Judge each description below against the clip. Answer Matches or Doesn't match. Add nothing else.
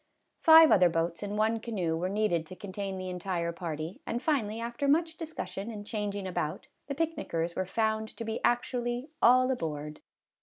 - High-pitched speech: Matches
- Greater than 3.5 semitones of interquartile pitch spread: Matches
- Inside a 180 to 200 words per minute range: Matches